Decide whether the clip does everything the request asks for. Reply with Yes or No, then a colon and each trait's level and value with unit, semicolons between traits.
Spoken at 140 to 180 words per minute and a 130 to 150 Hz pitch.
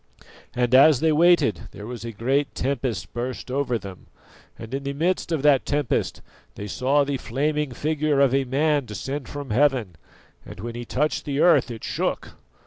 Yes: average, 175 wpm; low, 135 Hz